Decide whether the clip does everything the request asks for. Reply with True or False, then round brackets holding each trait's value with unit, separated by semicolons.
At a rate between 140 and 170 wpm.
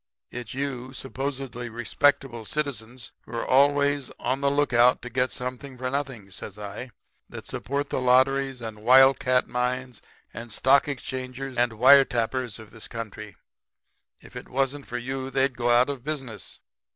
True (160 wpm)